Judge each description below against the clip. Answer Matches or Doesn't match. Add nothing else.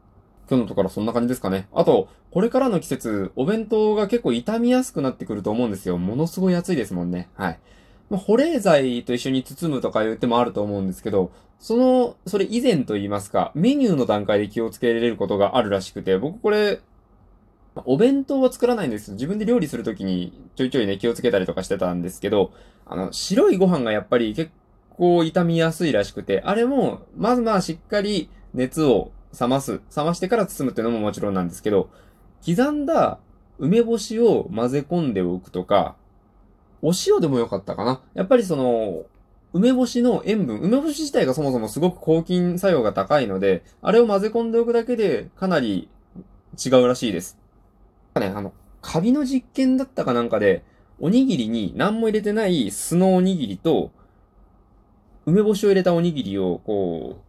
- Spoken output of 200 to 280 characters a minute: Doesn't match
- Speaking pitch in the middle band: Doesn't match